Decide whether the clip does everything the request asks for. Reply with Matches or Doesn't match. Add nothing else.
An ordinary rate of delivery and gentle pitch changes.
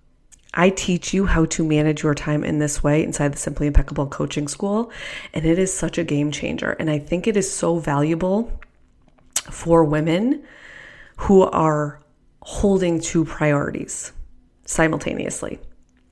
Doesn't match